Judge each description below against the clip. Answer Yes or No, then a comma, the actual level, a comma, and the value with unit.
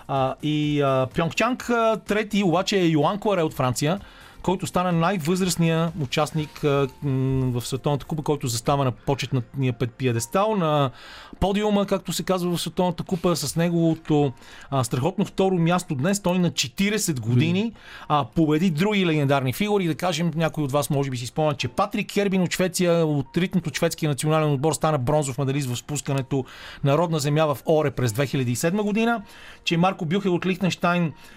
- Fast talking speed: Yes, fast, 170 wpm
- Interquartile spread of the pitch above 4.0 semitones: Yes, average, 4.4 semitones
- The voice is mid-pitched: Yes, medium, 160 Hz